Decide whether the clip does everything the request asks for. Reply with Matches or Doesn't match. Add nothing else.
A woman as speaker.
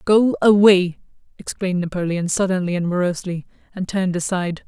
Matches